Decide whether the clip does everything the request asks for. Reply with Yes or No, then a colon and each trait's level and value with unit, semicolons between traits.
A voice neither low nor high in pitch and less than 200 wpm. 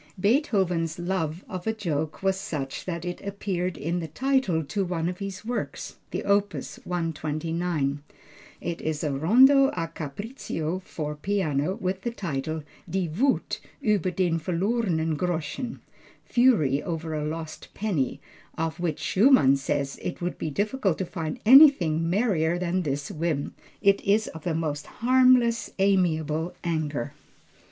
Yes: medium, 175 Hz; average, 140 wpm